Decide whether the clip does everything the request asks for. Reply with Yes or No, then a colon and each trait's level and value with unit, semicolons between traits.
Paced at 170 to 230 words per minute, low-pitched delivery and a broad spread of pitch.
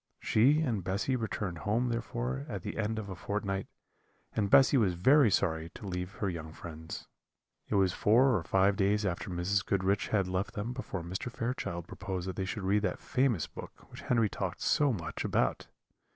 No: average, 190 wpm; low, 100 Hz; average, 3.7 semitones